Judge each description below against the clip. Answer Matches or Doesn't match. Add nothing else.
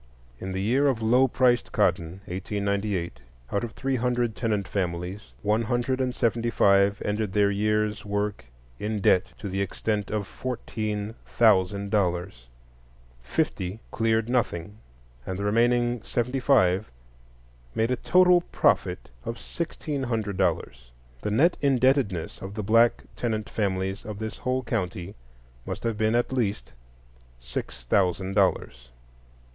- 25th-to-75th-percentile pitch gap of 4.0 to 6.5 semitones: Doesn't match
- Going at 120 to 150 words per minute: Matches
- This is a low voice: Matches